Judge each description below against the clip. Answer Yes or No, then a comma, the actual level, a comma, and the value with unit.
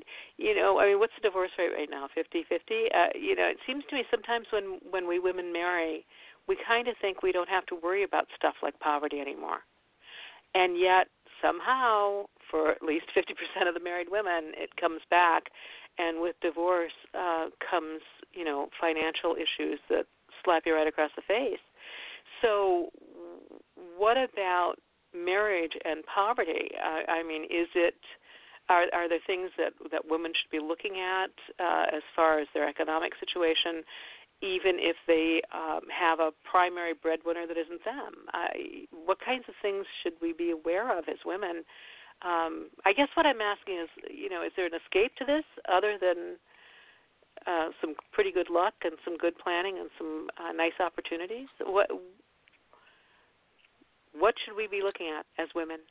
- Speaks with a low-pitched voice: No, medium, 175 Hz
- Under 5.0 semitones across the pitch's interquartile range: Yes, average, 4.3 semitones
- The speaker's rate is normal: Yes, average, 175 wpm